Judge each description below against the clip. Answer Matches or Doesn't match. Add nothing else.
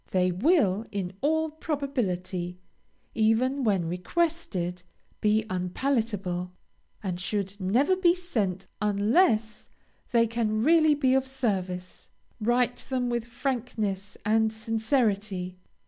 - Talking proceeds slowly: Matches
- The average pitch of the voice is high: Matches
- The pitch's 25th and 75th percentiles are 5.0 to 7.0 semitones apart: Matches